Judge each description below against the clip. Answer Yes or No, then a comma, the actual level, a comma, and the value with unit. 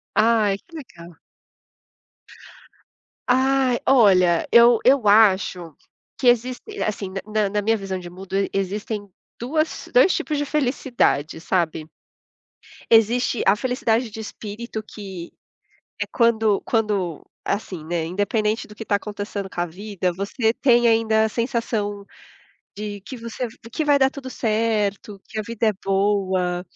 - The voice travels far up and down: No, average, 3.3 semitones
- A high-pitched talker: Yes, high, 215 Hz